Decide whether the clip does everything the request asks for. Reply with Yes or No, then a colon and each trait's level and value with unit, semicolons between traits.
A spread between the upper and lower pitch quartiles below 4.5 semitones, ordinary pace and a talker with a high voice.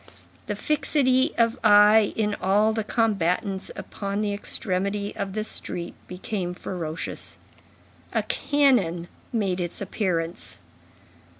No: average, 3.3 semitones; slow, 110 wpm; high, 205 Hz